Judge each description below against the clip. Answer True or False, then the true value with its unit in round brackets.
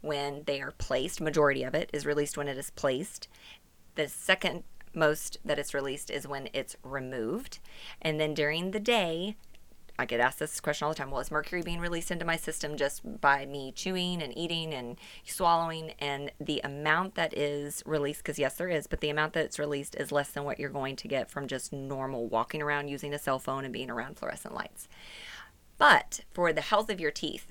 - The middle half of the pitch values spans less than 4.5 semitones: True (2.5 semitones)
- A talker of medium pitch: True (150 Hz)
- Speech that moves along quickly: True (210 wpm)